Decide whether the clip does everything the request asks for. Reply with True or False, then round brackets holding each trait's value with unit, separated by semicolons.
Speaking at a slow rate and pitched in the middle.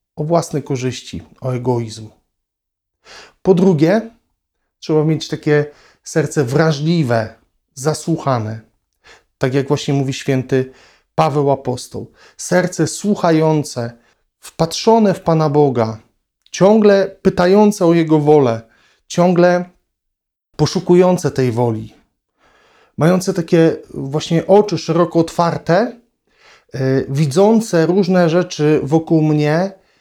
True (95 wpm; 155 Hz)